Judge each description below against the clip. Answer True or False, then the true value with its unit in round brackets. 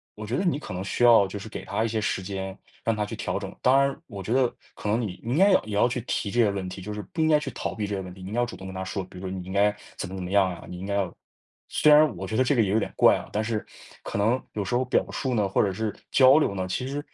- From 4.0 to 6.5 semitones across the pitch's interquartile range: True (4.3 semitones)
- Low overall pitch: True (105 Hz)